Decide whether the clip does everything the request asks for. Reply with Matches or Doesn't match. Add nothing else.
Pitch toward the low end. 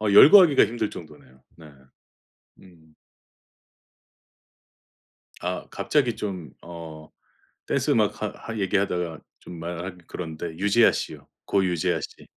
Matches